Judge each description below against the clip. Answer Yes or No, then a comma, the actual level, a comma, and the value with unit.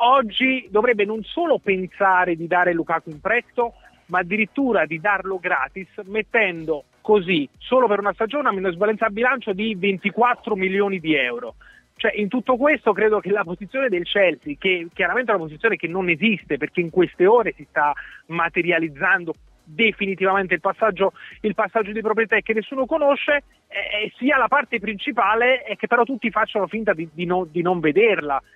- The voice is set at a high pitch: Yes, high, 205 Hz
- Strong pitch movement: No, average, 4.0 semitones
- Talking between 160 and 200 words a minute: Yes, fast, 170 wpm